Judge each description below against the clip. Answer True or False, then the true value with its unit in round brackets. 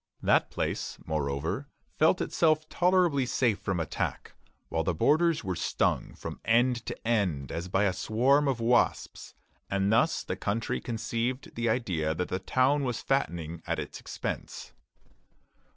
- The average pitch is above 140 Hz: False (115 Hz)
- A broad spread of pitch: True (7.0 semitones)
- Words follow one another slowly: False (150 wpm)